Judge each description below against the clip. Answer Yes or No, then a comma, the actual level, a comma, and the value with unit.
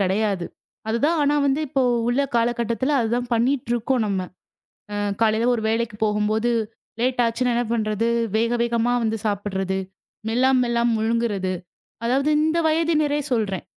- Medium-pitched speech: No, high, 235 Hz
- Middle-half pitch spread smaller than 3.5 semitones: Yes, average, 2.8 semitones